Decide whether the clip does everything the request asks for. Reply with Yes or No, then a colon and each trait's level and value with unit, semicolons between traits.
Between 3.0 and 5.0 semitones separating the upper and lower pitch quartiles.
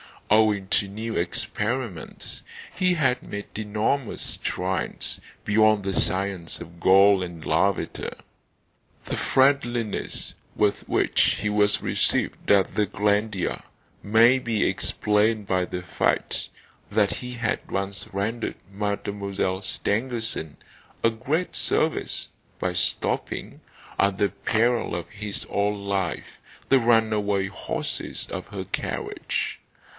No: narrow, 2.4 semitones